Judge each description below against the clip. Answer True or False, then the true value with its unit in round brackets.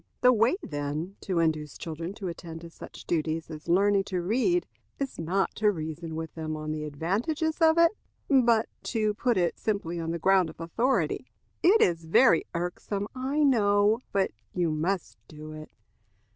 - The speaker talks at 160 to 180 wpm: True (170 wpm)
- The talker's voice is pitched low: False (180 Hz)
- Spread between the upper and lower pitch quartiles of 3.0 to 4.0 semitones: False (5.6 semitones)